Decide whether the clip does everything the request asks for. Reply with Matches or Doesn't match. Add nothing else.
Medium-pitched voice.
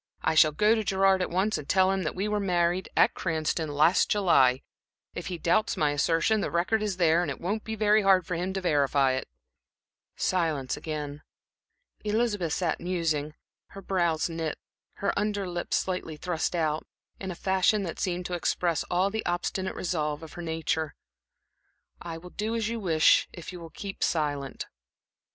Matches